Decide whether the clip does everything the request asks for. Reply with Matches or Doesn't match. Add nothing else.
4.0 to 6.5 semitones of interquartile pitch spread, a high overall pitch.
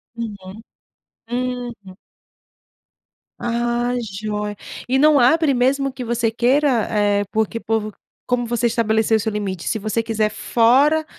Doesn't match